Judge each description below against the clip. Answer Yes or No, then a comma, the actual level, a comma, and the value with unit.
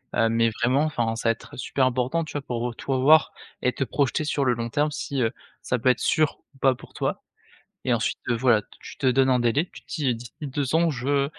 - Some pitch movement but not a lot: Yes, average, 3.2 semitones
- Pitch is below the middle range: Yes, low, 130 Hz